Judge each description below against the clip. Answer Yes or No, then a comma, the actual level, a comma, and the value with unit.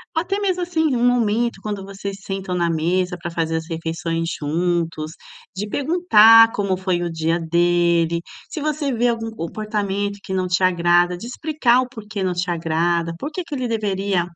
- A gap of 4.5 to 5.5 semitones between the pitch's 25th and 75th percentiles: Yes, average, 5.1 semitones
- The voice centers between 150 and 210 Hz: Yes, high, 190 Hz